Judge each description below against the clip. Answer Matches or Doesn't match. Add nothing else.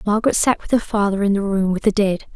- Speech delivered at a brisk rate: Matches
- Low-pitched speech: Doesn't match